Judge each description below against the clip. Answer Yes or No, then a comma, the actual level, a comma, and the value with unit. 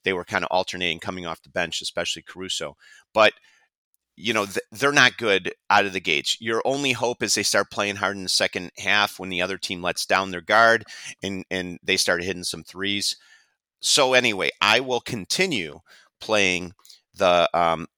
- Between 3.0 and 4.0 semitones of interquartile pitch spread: No, narrow, 2.4 semitones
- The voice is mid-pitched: No, very low, 95 Hz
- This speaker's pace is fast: No, average, 185 wpm